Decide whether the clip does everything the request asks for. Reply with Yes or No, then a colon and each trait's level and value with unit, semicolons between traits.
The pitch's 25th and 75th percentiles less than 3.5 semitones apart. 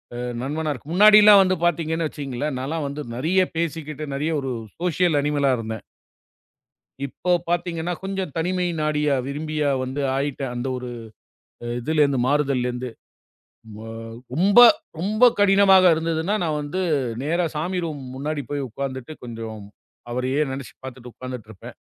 No: average, 4.2 semitones